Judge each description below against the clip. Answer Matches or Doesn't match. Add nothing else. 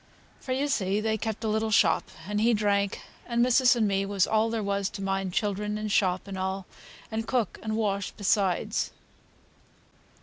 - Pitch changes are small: Matches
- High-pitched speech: Matches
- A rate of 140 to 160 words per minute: Doesn't match